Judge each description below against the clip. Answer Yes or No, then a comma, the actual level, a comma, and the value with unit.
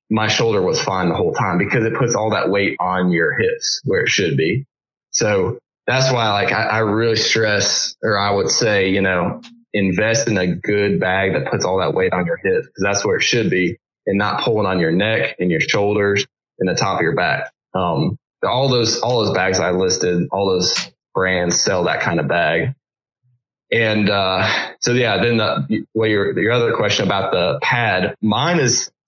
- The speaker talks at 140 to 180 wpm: No, fast, 205 wpm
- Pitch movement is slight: No, average, 4.7 semitones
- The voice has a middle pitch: No, low, 110 Hz